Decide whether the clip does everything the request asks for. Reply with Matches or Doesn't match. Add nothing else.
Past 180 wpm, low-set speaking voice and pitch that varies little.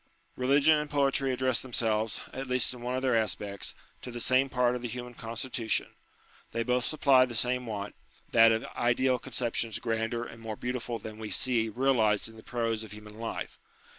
Matches